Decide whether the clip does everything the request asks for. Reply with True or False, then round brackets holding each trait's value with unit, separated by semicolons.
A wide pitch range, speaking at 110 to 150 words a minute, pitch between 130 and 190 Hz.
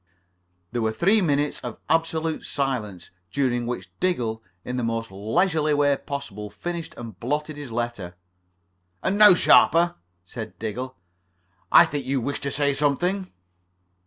True (5.8 semitones; 140 wpm; 140 Hz)